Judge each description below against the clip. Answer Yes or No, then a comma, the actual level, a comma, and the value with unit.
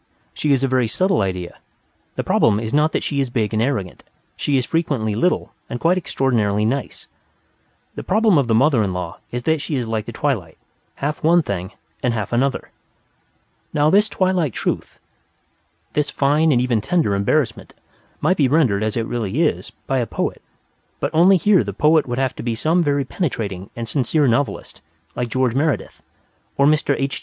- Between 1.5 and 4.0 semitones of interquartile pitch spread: No, wide, 5.4 semitones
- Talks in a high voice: No, low, 130 Hz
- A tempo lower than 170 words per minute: No, average, 185 wpm